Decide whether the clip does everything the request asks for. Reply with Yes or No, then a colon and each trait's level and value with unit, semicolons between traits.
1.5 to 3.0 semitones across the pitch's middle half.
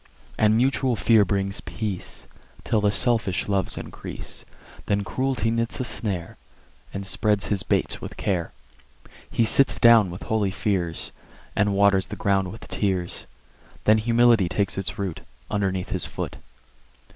Yes: average, 2.7 semitones